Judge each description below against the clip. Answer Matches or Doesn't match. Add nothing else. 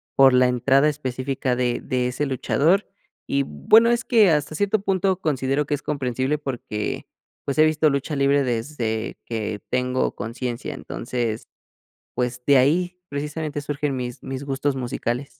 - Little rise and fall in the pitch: Doesn't match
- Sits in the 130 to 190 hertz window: Matches